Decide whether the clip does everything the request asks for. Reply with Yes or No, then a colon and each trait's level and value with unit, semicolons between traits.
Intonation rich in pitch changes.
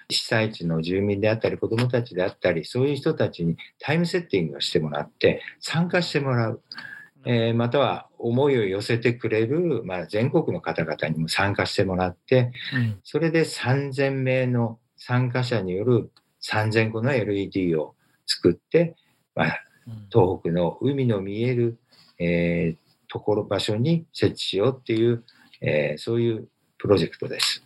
No: average, 4.5 semitones